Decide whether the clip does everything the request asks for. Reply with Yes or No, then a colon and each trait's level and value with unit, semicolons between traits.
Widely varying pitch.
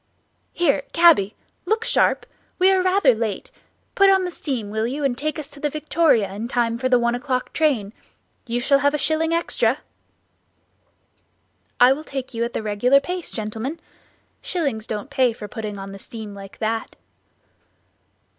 Yes: wide, 5.7 semitones